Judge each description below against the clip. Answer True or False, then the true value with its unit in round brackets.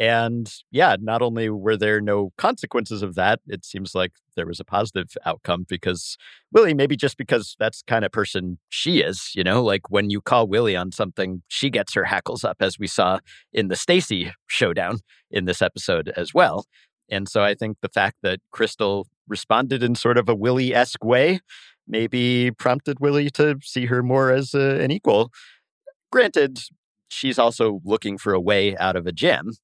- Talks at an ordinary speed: True (190 wpm)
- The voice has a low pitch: True (115 Hz)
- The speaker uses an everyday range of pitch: True (4.7 semitones)